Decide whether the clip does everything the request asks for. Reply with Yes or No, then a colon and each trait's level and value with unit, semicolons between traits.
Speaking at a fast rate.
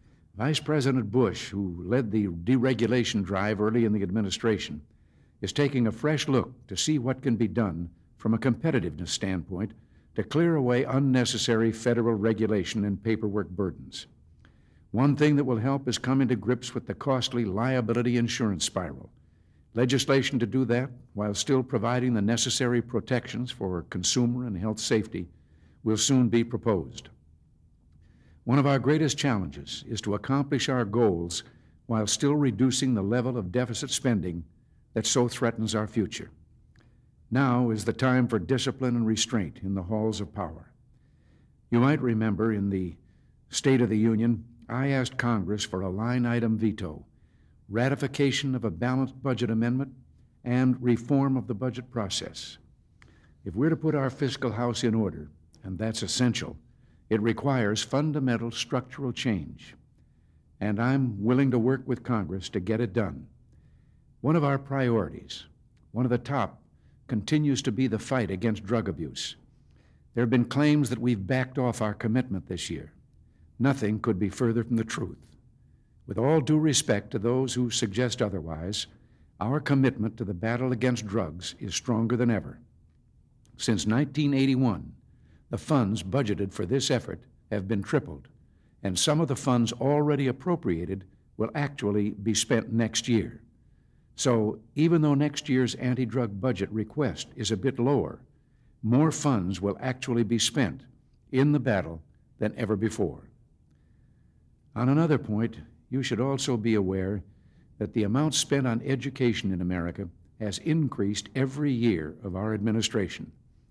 No: average, 155 wpm